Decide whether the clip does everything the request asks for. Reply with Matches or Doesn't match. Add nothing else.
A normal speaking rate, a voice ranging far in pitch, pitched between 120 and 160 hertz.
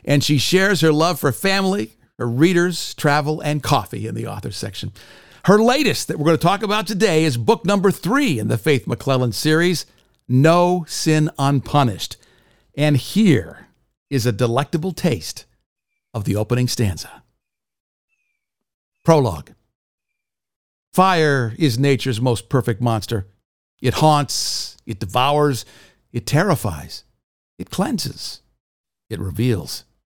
Doesn't match